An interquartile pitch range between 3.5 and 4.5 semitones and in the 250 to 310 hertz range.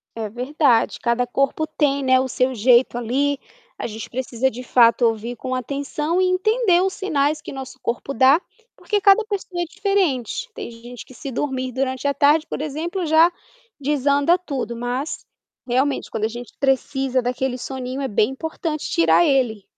Yes: average, 3.8 semitones; very high, 265 Hz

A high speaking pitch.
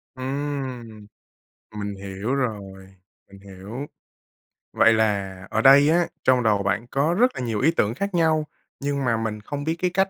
No: low, 120 Hz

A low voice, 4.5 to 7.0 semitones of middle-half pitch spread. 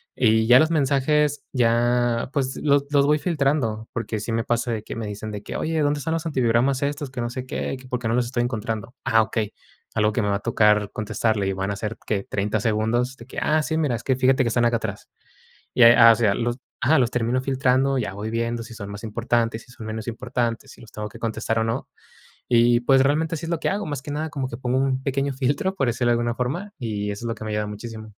No: low, 120 Hz; average, 3.3 semitones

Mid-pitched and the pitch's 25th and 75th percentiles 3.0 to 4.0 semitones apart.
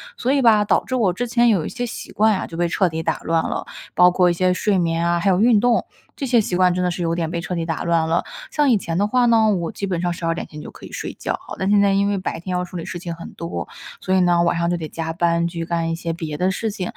Yes: medium, 180 Hz; average, 3.3 semitones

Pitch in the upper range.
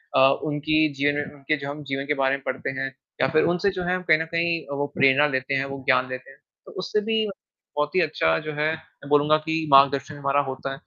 No: medium, 145 Hz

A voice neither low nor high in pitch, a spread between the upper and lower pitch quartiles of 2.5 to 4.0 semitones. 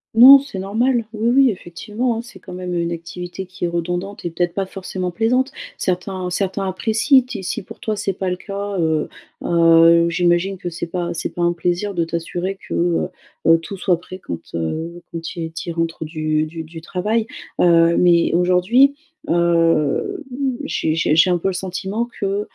Yes: medium, 180 Hz; average, 2.9 semitones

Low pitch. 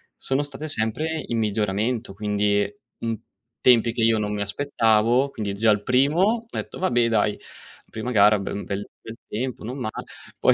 Yes: low, 115 Hz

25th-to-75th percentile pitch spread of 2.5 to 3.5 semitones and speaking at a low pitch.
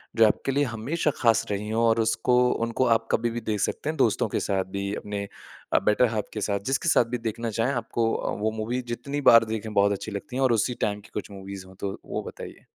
Yes: average, 2.8 semitones; low, 110 Hz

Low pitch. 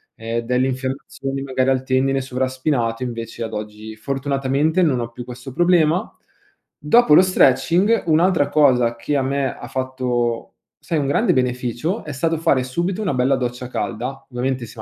Yes: low, 130 Hz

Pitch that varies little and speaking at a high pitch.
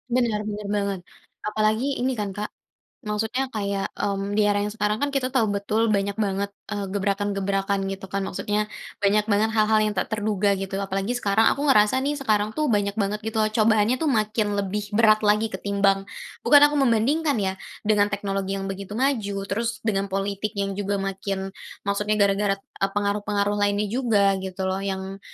Yes: narrow, 1.6 semitones; high, 205 Hz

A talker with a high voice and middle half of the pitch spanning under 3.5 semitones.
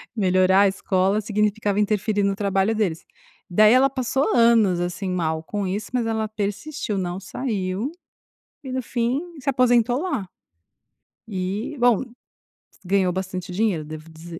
No: high, 205 Hz; average, 3.9 semitones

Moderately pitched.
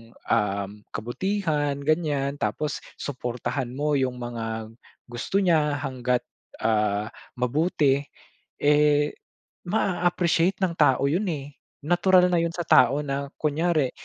Yes: medium, 145 Hz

